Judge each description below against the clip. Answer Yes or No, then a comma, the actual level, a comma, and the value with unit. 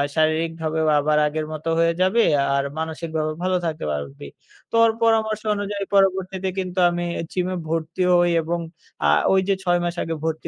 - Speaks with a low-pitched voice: No, medium, 170 Hz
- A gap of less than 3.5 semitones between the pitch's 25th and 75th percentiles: Yes, average, 2.9 semitones